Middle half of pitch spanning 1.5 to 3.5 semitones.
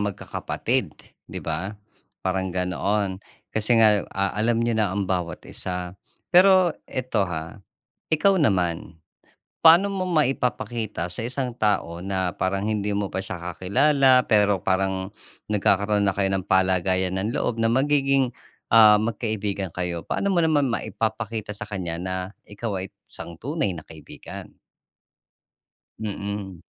No: average, 4.1 semitones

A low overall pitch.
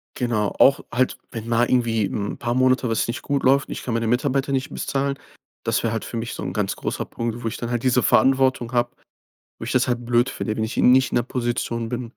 Yes: low, 120 Hz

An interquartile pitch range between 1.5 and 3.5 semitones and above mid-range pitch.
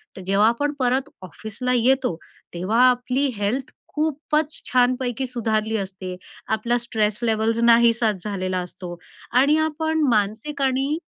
No: average, 4.0 semitones; high, 235 Hz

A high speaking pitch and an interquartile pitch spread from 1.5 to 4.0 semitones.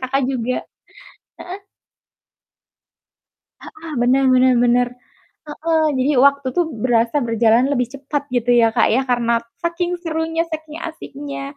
No: very high, 275 Hz; average, 4.4 semitones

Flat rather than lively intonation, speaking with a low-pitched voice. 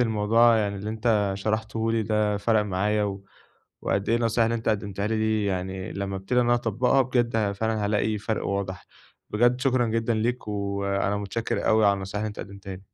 Yes: narrow, 2.3 semitones; low, 105 Hz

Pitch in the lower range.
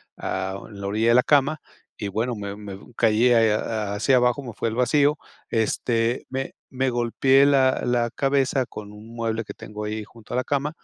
Yes: low, 115 Hz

